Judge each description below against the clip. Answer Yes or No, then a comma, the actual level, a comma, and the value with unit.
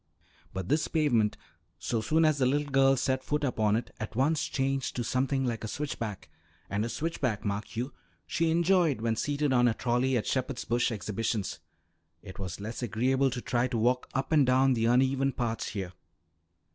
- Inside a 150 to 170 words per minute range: No, average, 185 wpm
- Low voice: Yes, low, 125 Hz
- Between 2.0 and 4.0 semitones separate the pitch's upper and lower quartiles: Yes, average, 3.4 semitones